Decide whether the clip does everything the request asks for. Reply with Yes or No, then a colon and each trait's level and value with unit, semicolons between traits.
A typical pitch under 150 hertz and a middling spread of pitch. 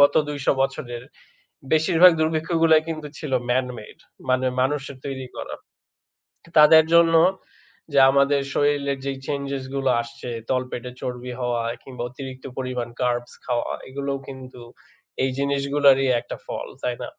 No: low, 135 Hz; narrow, 2.3 semitones